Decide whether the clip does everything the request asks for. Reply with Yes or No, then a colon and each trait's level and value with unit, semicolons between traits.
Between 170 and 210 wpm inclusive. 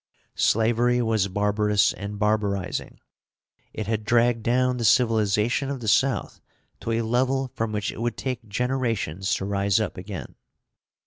No: average, 145 wpm